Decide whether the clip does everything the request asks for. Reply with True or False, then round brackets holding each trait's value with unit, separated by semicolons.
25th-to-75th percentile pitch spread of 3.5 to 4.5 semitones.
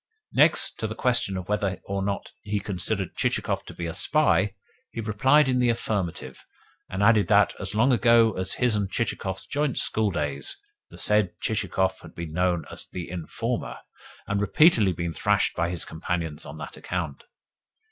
True (3.8 semitones)